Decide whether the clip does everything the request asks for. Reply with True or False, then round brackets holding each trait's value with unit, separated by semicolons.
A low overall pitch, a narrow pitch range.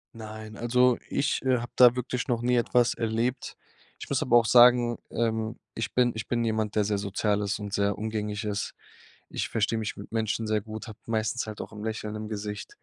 True (110 Hz; 2.0 semitones)